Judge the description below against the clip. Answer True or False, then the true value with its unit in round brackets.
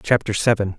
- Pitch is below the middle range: True (105 Hz)